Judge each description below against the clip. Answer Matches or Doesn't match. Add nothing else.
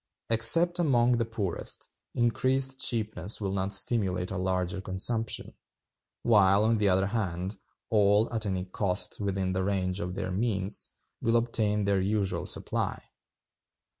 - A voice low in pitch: Matches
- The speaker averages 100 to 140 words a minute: Matches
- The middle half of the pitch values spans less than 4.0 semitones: Matches